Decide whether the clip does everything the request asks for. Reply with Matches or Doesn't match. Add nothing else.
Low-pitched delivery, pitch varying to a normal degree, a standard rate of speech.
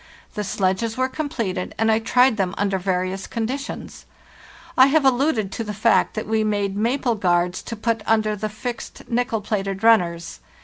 Doesn't match